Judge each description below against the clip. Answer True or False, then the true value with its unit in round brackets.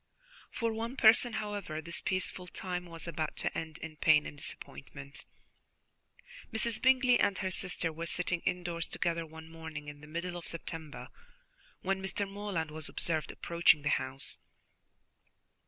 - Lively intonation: False (3.5 semitones)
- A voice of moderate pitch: True (170 Hz)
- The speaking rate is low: False (150 wpm)